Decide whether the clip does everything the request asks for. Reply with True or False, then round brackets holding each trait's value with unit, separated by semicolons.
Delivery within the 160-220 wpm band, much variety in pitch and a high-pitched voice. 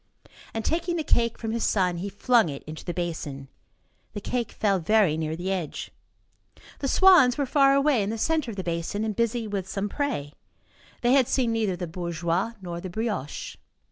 True (195 wpm; 5.7 semitones; 205 Hz)